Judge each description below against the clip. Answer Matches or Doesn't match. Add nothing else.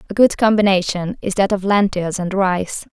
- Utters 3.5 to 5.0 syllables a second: Matches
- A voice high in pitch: Matches